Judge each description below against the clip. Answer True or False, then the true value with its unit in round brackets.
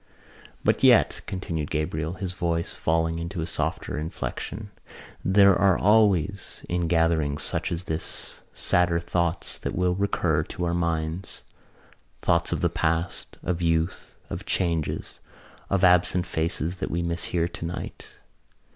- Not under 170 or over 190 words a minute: False (140 wpm)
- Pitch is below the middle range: True (85 Hz)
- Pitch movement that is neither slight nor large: False (1.8 semitones)